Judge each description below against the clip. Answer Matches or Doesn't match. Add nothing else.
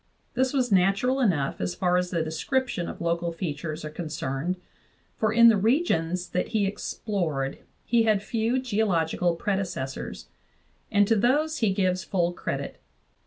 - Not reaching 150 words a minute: Doesn't match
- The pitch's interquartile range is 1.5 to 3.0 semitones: Doesn't match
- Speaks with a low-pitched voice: Doesn't match